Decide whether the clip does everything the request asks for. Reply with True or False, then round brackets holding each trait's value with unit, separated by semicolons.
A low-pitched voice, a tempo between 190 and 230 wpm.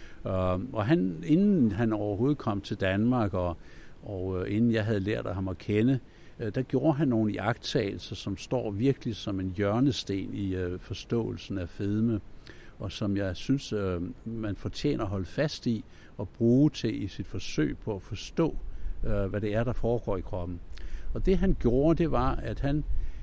False (105 Hz; 170 wpm)